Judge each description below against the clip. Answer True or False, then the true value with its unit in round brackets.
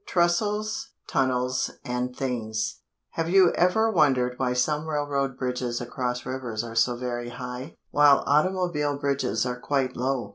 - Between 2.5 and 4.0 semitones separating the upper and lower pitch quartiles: True (3.5 semitones)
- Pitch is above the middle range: False (130 Hz)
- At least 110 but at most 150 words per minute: True (140 wpm)